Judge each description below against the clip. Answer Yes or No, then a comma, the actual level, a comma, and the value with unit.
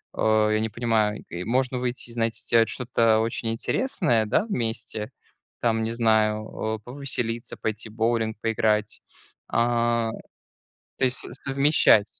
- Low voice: Yes, low, 115 Hz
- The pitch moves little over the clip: Yes, narrow, 1.7 semitones